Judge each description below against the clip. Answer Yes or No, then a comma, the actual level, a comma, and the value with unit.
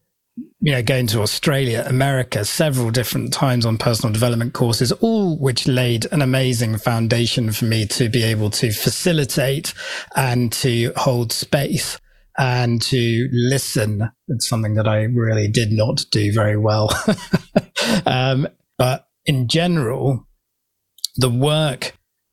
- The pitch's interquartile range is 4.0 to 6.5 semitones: No, average, 2.9 semitones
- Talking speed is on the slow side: Yes, slow, 130 wpm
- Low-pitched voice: Yes, low, 125 Hz